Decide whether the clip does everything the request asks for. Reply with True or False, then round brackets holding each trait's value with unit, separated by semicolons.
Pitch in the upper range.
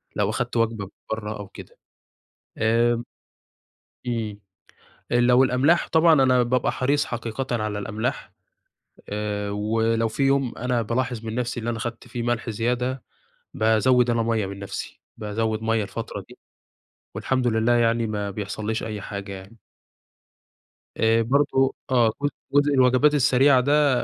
False (115 Hz)